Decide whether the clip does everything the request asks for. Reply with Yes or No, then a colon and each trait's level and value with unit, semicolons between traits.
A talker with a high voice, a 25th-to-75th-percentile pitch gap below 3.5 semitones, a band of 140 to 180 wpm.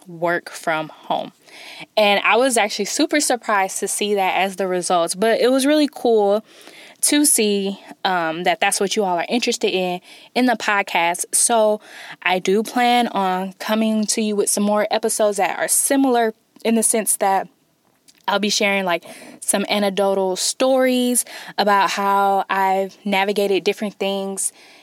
Yes: high, 205 Hz; average, 2.8 semitones; average, 160 wpm